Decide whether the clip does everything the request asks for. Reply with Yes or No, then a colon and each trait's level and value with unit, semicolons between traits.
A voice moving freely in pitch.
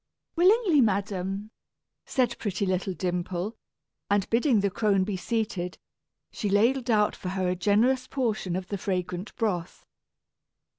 No: average, 3.8 semitones